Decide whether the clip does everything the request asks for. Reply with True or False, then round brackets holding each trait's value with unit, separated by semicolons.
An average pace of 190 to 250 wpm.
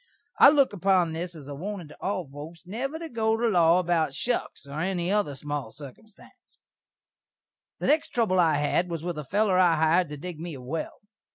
True (200 wpm)